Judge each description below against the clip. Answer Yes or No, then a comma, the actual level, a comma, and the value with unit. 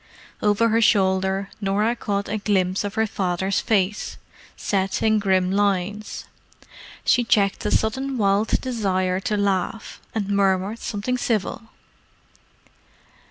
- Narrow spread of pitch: Yes, narrow, 2.3 semitones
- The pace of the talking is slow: Yes, slow, 120 wpm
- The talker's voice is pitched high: Yes, high, 200 Hz